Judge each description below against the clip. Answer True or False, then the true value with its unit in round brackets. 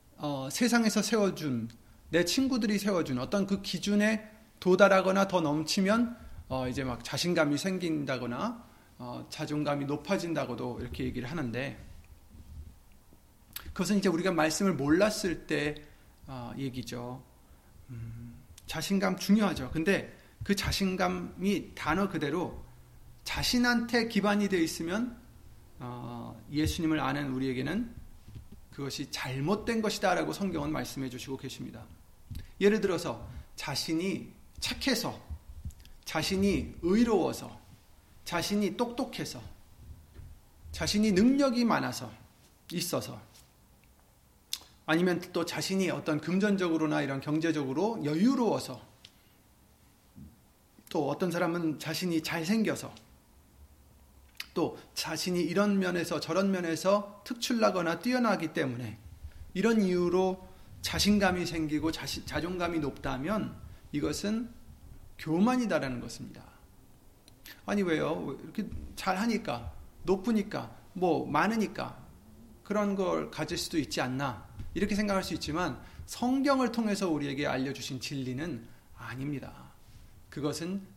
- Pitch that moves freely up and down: True (8.2 semitones)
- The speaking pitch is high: False (160 Hz)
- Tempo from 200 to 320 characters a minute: True (260 characters per minute)